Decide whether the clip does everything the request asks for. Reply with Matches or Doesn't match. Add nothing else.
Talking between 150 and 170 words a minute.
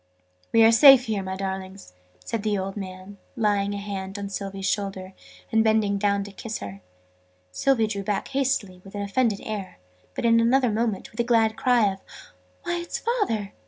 Doesn't match